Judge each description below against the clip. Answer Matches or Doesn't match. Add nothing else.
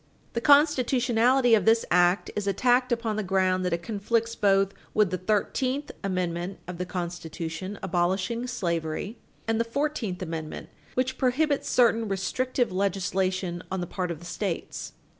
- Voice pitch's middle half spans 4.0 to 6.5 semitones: Matches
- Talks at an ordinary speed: Matches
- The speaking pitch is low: Doesn't match